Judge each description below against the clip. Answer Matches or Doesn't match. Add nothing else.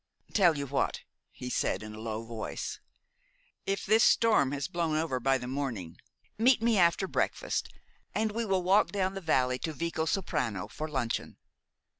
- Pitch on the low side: Doesn't match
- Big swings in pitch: Matches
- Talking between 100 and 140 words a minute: Doesn't match